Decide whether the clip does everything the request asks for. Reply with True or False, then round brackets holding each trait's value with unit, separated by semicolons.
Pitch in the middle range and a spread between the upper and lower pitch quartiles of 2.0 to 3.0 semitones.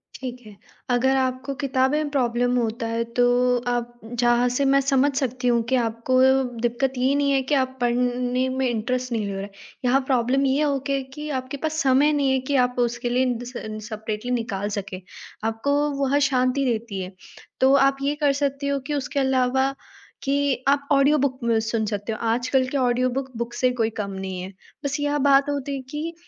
False (255 Hz; 2.5 semitones)